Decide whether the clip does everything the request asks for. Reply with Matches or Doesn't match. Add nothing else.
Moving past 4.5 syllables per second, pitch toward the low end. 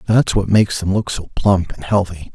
Matches